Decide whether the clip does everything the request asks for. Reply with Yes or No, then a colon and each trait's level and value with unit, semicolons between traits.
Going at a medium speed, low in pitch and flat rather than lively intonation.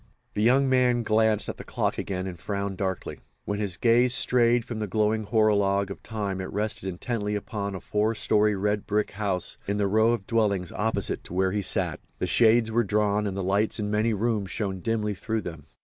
No: fast, 210 wpm; low, 105 Hz; narrow, 2.2 semitones